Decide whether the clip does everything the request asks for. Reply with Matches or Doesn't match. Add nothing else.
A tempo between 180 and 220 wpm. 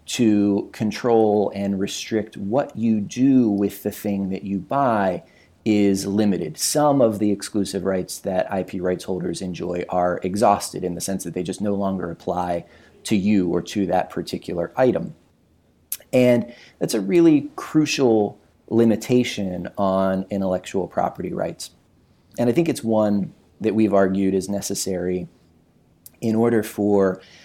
Doesn't match